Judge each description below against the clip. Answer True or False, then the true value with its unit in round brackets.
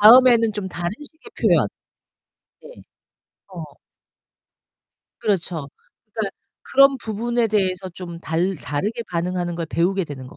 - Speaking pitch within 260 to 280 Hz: False (190 Hz)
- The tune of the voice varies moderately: True (4.8 semitones)